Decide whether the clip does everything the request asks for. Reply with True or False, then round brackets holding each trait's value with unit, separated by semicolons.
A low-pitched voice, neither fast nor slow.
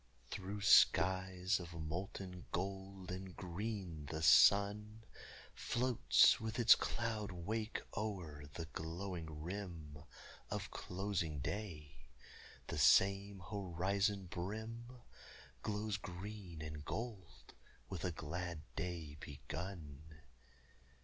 False (95 Hz; 95 wpm)